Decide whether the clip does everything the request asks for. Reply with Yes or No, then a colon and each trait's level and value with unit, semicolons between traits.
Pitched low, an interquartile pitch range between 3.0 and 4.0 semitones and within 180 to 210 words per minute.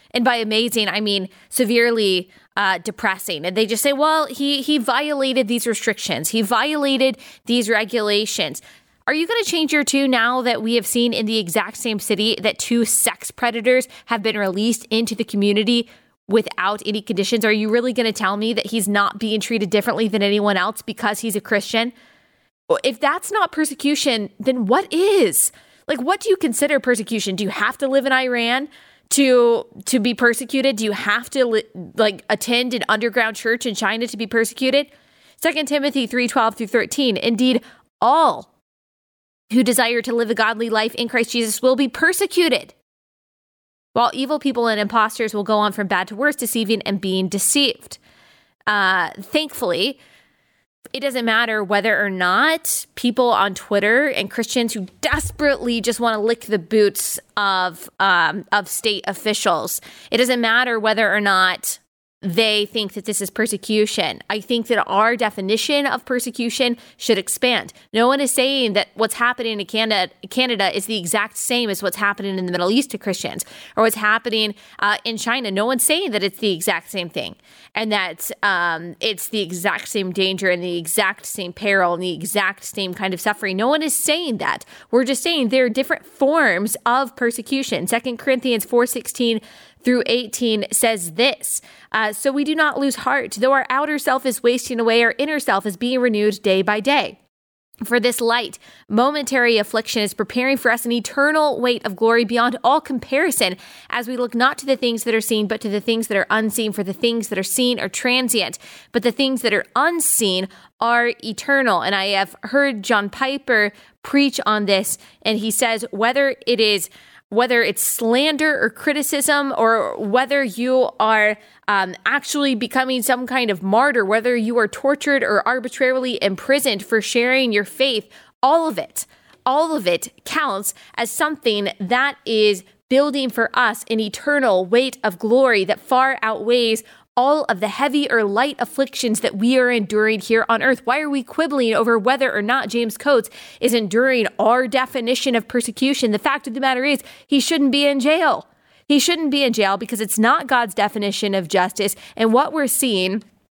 No: high, 235 Hz; average, 3.7 semitones; average, 185 wpm